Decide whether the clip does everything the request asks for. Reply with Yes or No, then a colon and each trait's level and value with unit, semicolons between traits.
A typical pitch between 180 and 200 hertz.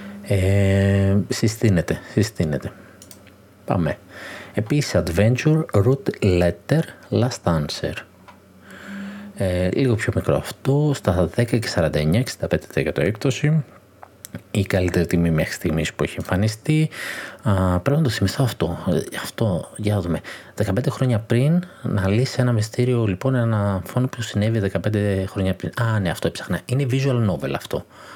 No: low, 105 Hz